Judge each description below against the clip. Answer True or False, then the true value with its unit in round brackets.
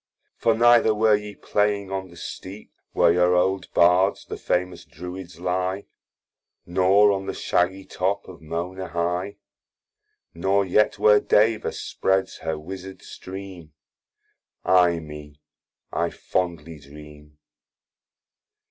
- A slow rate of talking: True (120 wpm)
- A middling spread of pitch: False (2.3 semitones)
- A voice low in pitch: True (95 Hz)